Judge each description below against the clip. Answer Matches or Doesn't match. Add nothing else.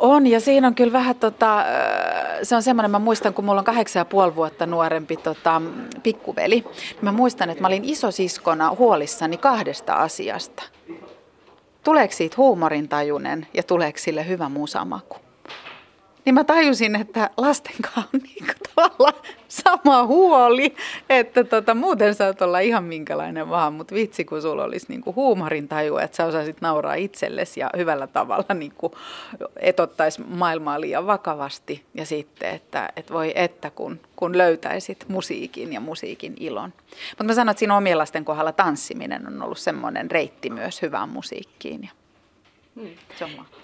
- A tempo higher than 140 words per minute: Matches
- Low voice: Doesn't match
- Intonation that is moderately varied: Doesn't match